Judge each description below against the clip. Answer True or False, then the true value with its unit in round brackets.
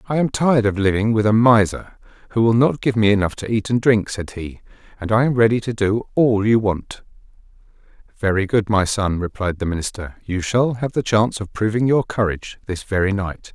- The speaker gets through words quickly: True (215 wpm)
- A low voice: True (110 Hz)